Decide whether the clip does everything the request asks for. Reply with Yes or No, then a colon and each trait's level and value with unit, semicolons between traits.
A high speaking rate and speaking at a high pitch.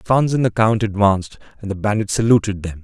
No: fast, 210 wpm; low, 105 Hz